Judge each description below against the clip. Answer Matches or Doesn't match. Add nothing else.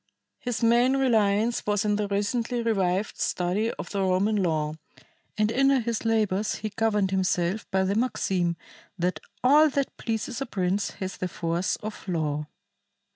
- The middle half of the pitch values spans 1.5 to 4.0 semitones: Matches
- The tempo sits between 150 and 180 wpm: Matches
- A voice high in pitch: Matches